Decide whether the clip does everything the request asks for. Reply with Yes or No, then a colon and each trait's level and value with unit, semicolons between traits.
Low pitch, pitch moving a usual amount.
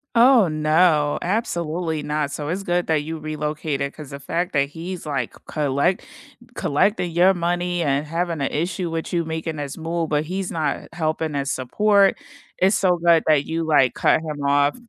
No: medium, 160 Hz; average, 3.0 semitones